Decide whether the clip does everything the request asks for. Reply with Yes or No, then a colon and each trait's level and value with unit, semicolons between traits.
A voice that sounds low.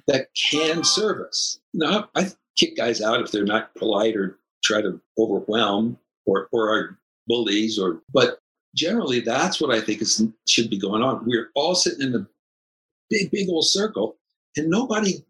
Yes: low, 130 Hz